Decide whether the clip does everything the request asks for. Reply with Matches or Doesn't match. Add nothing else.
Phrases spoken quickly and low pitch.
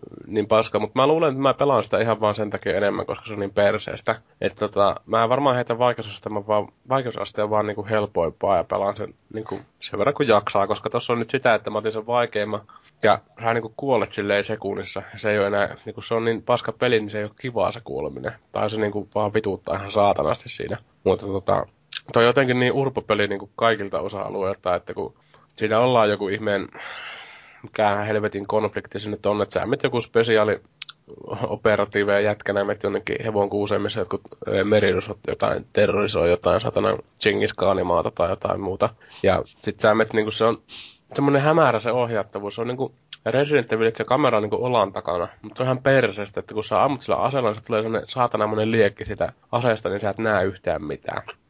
Matches